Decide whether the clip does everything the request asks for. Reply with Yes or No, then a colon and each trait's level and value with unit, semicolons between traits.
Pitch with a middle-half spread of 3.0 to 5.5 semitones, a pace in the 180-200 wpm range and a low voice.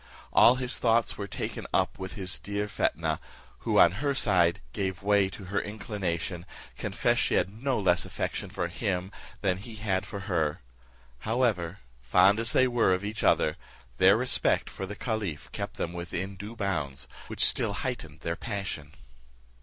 No: average, 3.4 semitones; average, 170 wpm; low, 100 Hz